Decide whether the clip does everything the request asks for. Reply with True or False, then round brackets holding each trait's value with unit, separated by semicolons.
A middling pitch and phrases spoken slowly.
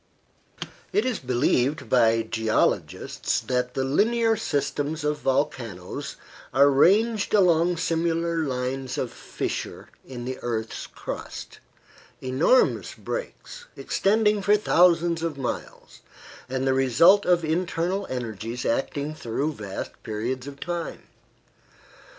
True (145 Hz; 110 wpm)